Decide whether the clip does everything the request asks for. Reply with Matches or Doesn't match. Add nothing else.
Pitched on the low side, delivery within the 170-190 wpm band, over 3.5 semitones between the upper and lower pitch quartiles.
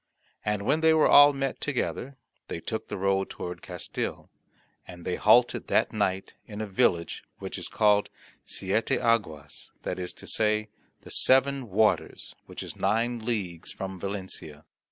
Doesn't match